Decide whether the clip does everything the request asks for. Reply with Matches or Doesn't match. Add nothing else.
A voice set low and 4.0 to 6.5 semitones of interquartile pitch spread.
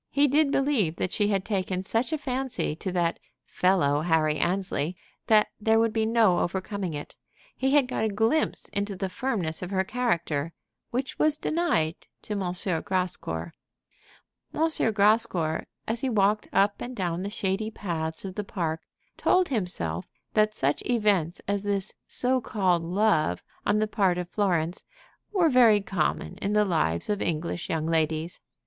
Doesn't match